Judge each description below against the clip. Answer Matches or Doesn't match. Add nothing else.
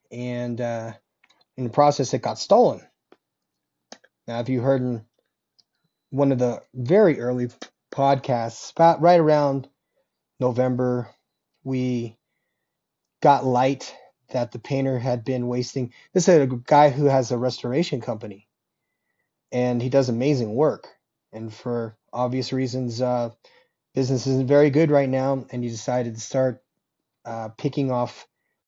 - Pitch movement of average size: Doesn't match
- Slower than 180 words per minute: Matches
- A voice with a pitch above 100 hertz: Matches